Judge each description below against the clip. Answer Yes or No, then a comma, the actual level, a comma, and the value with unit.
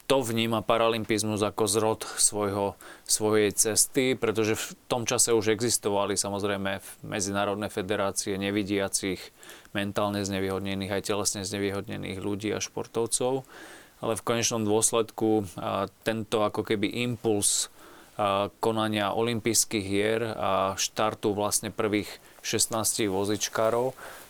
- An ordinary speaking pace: No, slow, 105 wpm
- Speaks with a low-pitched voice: Yes, low, 105 Hz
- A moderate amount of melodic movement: No, narrow, 2.1 semitones